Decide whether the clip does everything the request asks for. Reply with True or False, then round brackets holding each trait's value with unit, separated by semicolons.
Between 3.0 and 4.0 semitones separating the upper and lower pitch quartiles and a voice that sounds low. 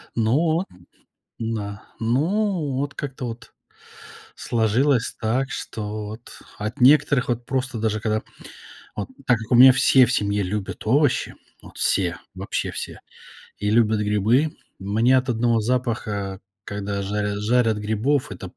True (3.7 semitones; 115 Hz)